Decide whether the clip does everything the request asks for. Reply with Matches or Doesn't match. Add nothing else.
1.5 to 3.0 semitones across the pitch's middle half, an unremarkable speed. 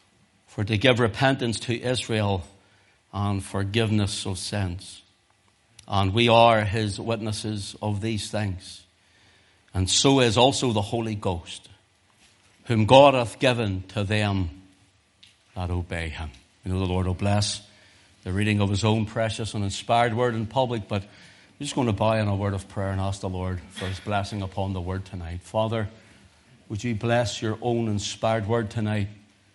Matches